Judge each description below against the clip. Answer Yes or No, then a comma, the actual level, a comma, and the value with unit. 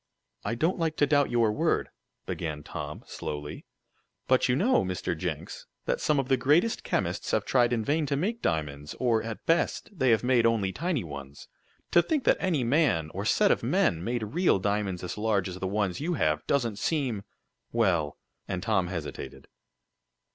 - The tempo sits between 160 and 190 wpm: Yes, average, 185 wpm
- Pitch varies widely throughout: Yes, wide, 8.1 semitones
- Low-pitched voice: Yes, low, 115 Hz